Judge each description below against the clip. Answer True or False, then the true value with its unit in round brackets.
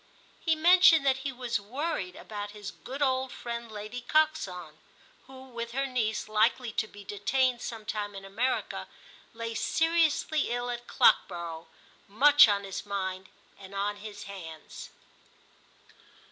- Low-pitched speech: False (230 Hz)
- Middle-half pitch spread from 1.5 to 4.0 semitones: False (4.6 semitones)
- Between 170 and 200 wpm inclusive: False (140 wpm)